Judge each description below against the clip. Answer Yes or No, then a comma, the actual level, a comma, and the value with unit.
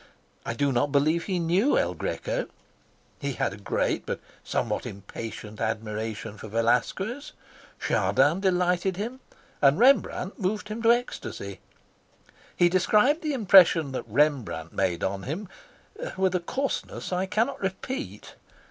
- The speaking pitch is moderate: Yes, medium, 175 Hz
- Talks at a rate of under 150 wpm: Yes, slow, 135 wpm